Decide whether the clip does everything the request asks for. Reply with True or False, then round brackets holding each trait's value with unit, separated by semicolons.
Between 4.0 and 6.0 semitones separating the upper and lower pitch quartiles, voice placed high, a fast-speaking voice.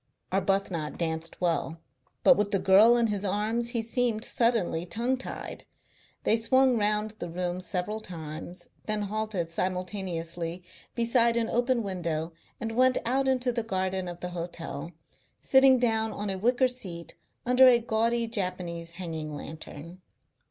False (5.1 semitones; 205 Hz; 145 wpm)